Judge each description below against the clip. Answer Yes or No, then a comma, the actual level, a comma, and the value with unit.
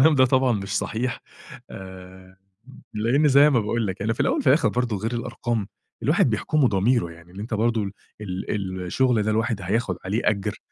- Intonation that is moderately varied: Yes, average, 4.1 semitones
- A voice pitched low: Yes, low, 110 Hz